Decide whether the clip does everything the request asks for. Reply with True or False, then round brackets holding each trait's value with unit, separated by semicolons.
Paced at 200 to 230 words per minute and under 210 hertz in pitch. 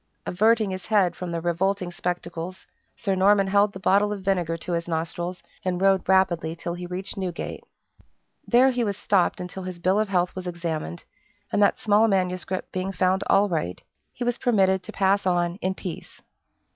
False (185 wpm; 185 Hz)